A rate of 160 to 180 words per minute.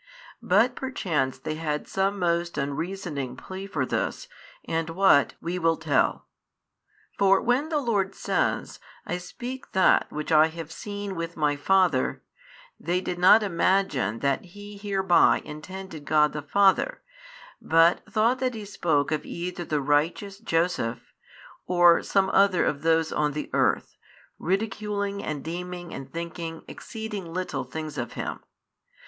No: average, 140 wpm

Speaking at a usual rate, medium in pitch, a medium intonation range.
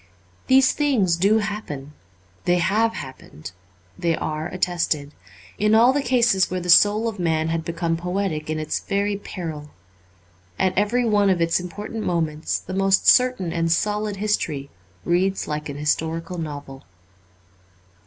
Yes: average, 145 wpm; medium, 180 Hz; average, 4.5 semitones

